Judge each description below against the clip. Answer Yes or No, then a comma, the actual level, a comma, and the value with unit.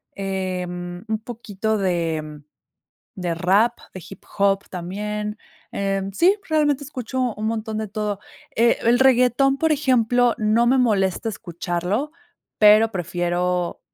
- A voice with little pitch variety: No, average, 4.7 semitones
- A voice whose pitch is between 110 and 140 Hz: No, high, 210 Hz